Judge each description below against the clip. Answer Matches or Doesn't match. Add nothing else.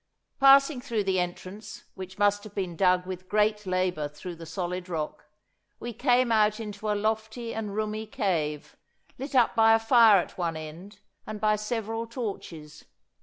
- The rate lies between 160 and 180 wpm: Matches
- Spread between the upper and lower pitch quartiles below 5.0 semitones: Matches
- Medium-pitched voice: Doesn't match